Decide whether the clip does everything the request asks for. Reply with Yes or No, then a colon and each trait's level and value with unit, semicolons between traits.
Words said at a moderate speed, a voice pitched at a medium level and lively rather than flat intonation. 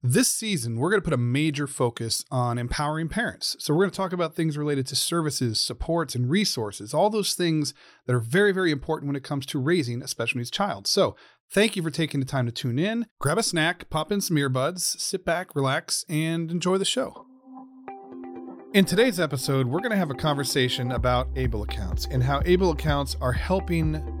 No: fast, 210 wpm; medium, 150 Hz; wide, 6.2 semitones